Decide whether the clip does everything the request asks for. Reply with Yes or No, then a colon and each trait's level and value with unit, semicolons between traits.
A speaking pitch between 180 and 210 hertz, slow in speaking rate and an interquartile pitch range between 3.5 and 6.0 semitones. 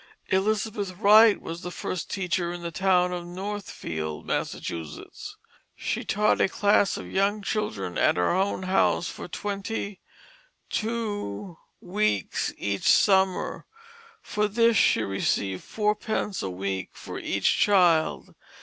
Yes: high, 190 Hz; slow, 125 wpm; average, 3.9 semitones